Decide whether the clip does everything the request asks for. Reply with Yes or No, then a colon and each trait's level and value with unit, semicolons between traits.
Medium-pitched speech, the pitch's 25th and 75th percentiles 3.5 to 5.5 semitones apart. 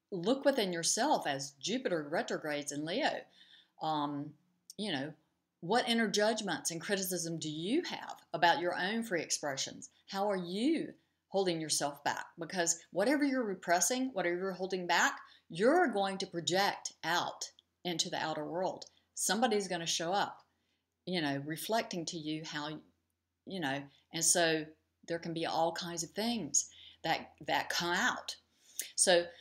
Yes: medium, 175 Hz; average, 4.0 semitones